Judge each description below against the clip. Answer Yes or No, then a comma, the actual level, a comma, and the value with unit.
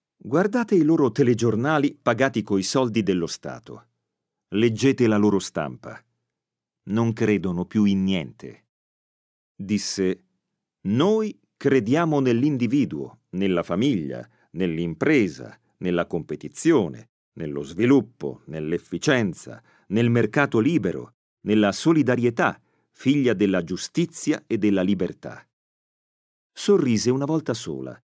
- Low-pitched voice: Yes, low, 115 Hz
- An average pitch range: No, wide, 6.9 semitones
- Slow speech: Yes, slow, 95 wpm